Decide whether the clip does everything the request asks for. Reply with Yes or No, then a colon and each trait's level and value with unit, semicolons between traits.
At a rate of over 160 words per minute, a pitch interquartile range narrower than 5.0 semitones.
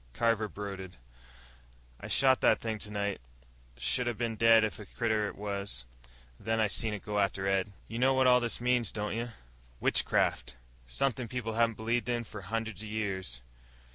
Yes: average, 175 wpm; narrow, 2.5 semitones